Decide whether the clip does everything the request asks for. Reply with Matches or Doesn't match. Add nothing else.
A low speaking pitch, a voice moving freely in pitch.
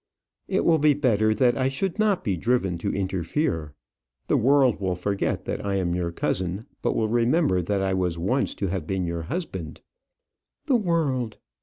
Matches